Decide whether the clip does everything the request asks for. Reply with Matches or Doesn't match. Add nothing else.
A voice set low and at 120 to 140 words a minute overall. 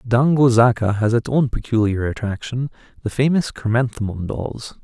Matches